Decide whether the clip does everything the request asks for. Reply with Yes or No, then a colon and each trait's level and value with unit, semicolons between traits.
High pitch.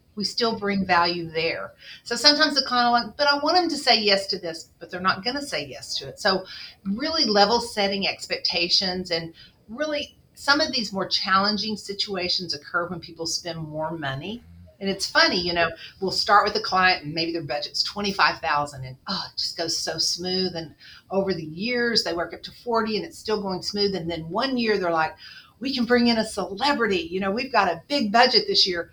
Yes: high, 195 Hz